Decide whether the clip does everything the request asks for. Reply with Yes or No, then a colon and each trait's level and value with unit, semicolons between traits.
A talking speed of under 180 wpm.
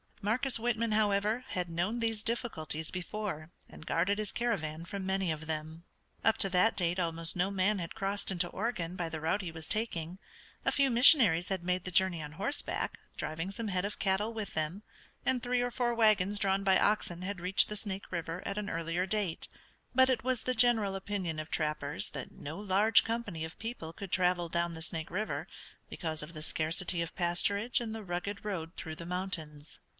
No: average, 200 wpm